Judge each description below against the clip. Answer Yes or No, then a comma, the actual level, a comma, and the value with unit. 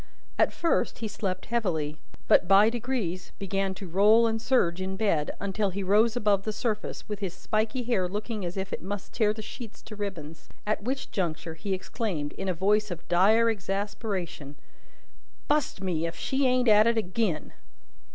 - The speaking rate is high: No, average, 180 wpm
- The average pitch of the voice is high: Yes, high, 200 Hz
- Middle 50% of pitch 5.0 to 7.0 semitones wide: No, average, 3.3 semitones